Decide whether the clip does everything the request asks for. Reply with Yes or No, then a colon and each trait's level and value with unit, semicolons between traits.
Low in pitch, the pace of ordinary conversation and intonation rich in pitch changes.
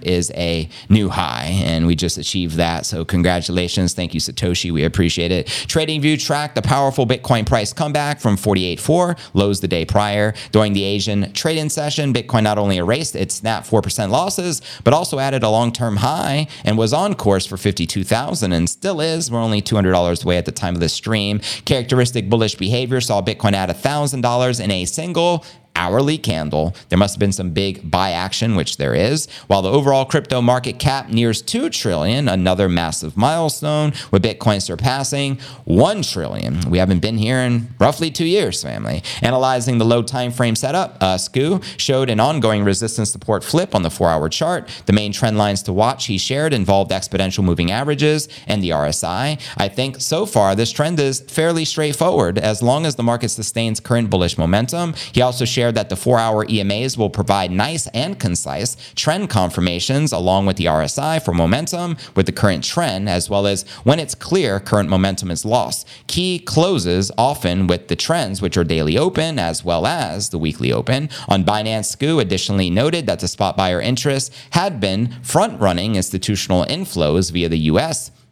Yes: low, 110 Hz; average, 185 wpm; wide, 6.2 semitones